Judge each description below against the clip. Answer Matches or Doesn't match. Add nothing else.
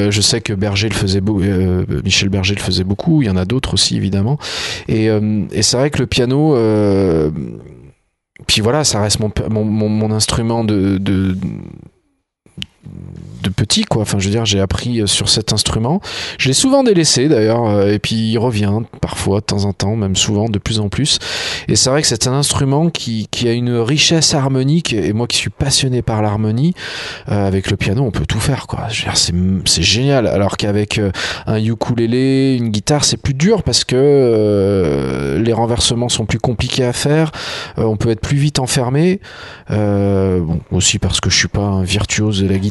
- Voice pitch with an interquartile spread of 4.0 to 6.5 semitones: Matches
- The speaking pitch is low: Matches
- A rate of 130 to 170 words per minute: Doesn't match